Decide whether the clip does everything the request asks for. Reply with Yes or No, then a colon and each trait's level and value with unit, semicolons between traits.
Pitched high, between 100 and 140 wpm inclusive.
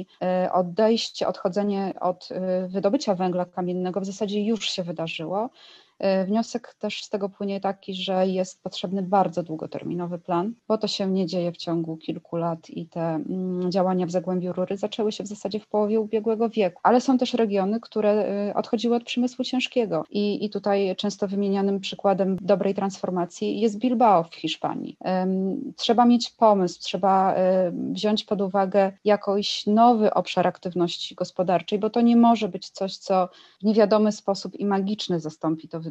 No: high, 195 Hz; average, 155 wpm